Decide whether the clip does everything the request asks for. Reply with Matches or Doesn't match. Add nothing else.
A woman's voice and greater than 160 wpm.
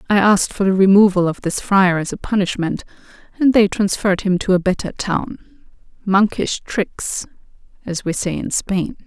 Matches